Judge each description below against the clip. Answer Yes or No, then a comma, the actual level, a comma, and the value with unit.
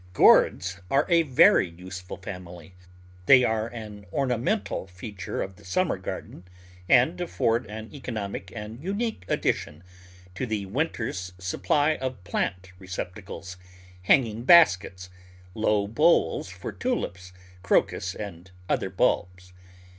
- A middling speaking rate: No, slow, 120 wpm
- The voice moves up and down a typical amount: No, wide, 5.7 semitones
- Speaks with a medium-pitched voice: No, low, 100 Hz